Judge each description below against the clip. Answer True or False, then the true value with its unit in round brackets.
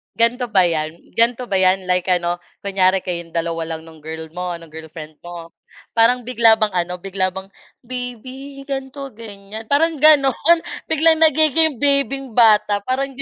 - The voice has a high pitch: True (220 Hz)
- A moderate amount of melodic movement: False (7.1 semitones)